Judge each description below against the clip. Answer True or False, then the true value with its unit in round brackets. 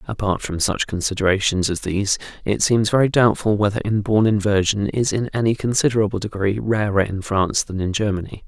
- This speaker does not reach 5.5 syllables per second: False (5.9 syllables/s)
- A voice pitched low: True (105 Hz)